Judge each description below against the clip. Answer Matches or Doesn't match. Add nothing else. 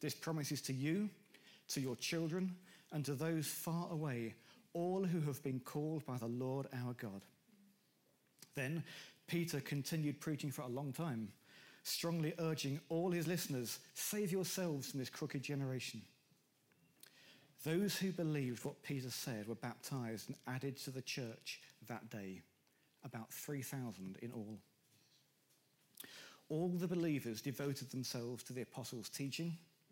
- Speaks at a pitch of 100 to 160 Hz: Matches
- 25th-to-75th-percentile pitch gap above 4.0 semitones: Matches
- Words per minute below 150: Matches